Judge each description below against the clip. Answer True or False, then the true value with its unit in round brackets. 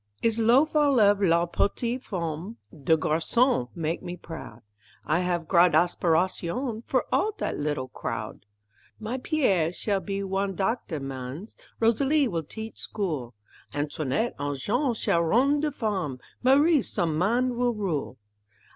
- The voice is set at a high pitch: True (195 Hz)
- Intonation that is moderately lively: False (6.7 semitones)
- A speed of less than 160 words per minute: True (140 wpm)